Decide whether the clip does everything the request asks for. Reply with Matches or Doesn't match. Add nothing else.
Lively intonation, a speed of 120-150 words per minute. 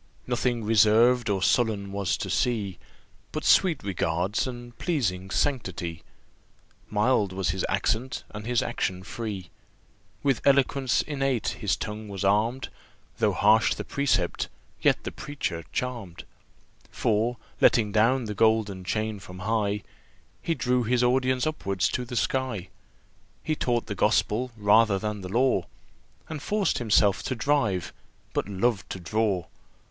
Doesn't match